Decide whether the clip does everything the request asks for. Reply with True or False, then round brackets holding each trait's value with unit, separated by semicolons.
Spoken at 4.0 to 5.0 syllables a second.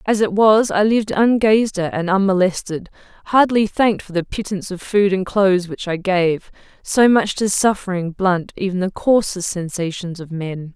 True (4.9 syllables/s)